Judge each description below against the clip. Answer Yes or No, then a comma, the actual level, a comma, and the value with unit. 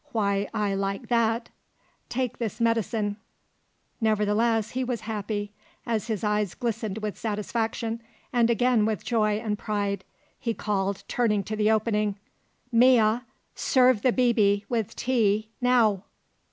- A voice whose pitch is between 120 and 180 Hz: No, high, 220 Hz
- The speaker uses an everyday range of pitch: No, narrow, 2.1 semitones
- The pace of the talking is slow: Yes, slow, 130 wpm